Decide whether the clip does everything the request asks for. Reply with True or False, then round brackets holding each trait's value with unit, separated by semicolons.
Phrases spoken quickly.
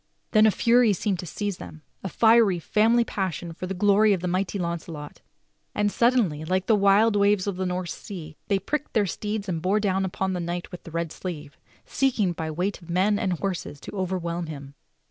True (215 wpm)